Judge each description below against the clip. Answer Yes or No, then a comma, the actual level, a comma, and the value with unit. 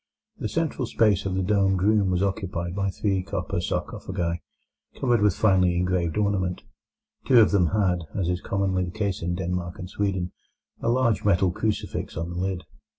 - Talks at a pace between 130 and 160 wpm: No, average, 175 wpm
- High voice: No, very low, 95 Hz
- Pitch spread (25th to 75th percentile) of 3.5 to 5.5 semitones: No, narrow, 2.5 semitones